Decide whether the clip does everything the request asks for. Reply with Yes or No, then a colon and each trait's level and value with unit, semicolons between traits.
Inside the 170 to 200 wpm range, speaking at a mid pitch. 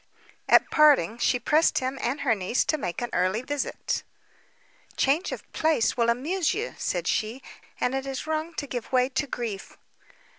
No: average, 180 wpm; very high, 260 Hz